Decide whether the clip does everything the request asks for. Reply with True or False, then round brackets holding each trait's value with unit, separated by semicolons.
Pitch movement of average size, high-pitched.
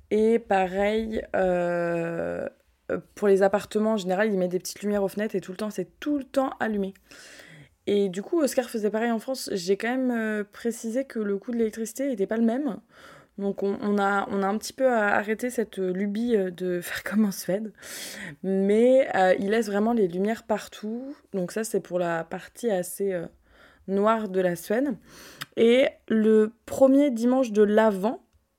True (3.1 semitones; 210 Hz)